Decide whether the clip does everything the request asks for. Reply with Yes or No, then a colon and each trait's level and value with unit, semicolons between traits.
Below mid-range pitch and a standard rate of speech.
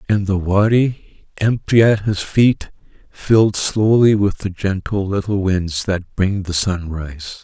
Yes: low, 100 Hz; average, 145 wpm